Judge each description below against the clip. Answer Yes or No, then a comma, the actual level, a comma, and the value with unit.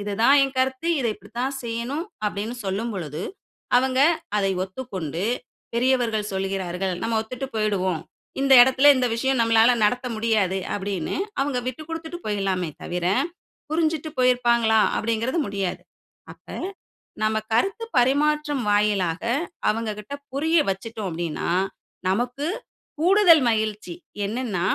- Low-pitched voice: No, high, 230 Hz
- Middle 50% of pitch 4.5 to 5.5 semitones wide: Yes, average, 4.9 semitones